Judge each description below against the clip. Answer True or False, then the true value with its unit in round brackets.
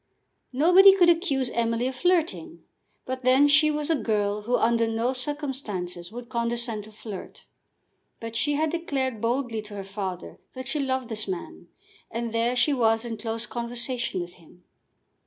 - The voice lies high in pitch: True (235 Hz)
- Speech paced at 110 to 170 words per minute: True (165 wpm)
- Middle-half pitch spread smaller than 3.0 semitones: False (3.8 semitones)